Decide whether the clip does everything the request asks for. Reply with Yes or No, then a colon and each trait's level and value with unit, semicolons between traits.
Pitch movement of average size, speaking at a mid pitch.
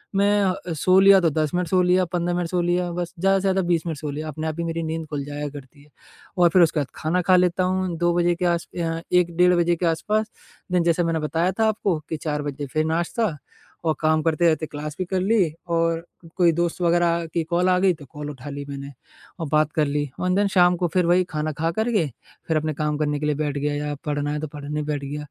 Yes: average, 3.0 semitones; medium, 165 Hz